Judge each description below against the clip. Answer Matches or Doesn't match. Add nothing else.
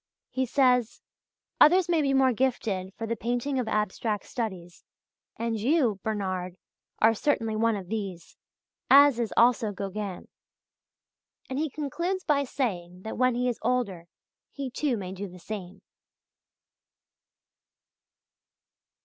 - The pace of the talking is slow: Matches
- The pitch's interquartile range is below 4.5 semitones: Doesn't match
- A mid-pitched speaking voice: Doesn't match